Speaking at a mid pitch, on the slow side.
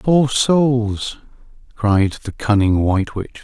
No: low, 115 Hz; slow, 120 wpm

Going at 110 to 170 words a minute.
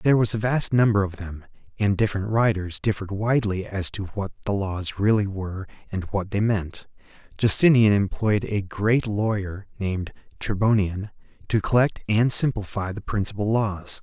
Yes: average, 165 wpm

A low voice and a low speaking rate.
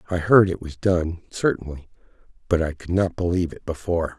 No: very low, 85 Hz; average, 185 wpm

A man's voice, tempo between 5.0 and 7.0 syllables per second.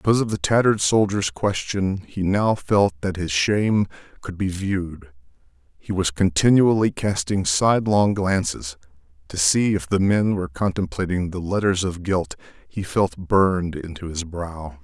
No: male; 4.7 syllables/s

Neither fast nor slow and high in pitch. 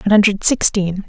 Yes: average, 165 wpm; high, 200 Hz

